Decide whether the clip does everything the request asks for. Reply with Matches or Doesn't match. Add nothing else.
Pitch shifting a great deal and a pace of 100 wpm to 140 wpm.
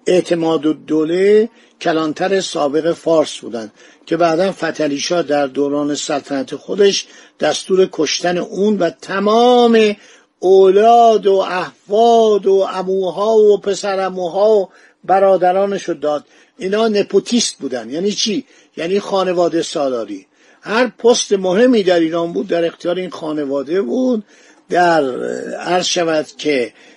Doesn't match